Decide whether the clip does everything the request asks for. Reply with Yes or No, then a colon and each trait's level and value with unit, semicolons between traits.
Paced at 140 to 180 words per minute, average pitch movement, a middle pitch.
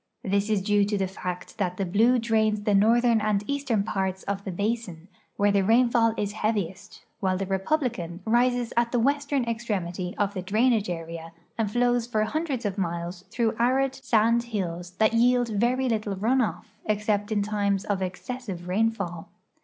No: average, 175 wpm; average, 3.6 semitones; high, 210 Hz